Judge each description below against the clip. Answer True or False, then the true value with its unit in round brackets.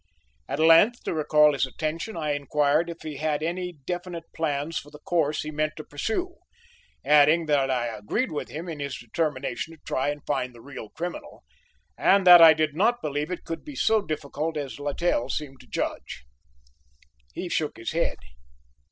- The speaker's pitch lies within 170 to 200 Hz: False (155 Hz)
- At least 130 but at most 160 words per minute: False (180 wpm)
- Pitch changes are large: False (2.8 semitones)